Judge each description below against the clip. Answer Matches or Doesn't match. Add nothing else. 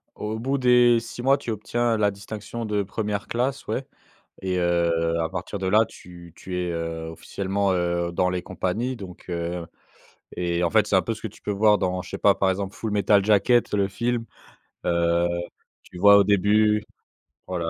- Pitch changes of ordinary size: Matches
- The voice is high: Doesn't match